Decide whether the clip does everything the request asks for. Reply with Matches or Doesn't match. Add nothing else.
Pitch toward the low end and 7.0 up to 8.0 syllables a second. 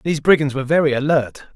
Doesn't match